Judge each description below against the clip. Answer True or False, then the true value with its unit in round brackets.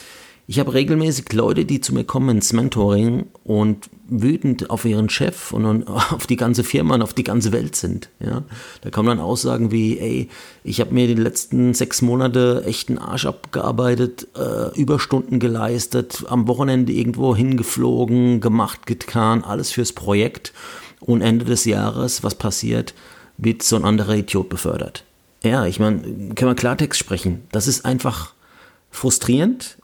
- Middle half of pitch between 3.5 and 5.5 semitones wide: False (2.6 semitones)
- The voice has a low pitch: True (120 Hz)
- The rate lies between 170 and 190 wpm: False (155 wpm)